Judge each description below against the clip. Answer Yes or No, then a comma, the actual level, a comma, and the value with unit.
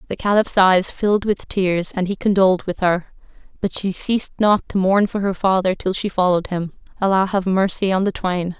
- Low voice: No, high, 190 Hz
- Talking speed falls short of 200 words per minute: No, fast, 205 wpm